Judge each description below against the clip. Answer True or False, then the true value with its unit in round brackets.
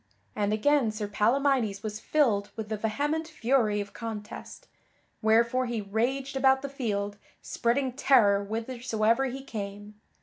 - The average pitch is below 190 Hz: False (230 Hz)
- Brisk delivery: False (135 wpm)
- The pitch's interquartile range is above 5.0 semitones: False (4.2 semitones)